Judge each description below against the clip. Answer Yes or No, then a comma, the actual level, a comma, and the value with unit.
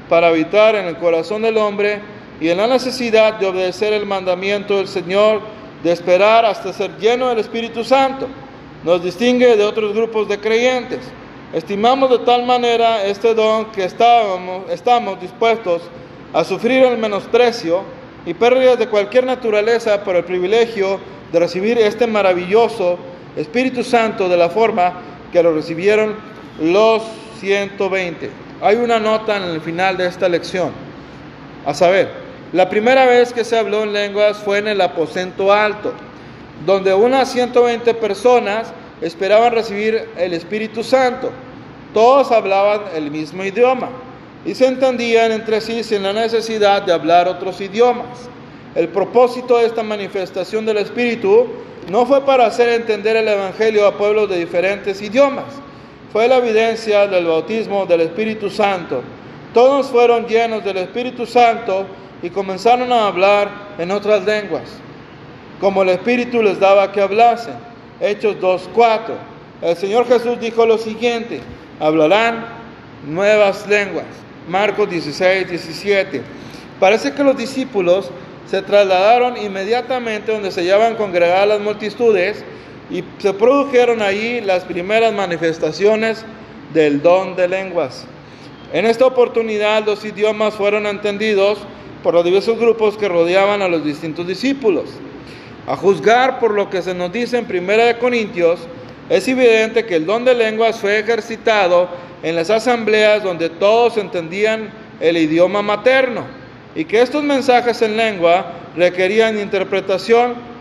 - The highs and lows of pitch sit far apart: No, average, 3.7 semitones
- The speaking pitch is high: Yes, high, 210 Hz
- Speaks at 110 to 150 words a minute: Yes, average, 140 wpm